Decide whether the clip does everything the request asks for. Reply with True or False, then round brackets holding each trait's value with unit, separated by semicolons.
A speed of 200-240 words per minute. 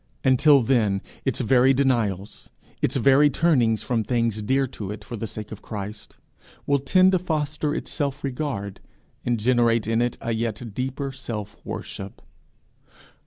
False (155 wpm)